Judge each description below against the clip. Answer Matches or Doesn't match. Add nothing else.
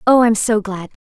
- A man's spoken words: Doesn't match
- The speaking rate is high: Matches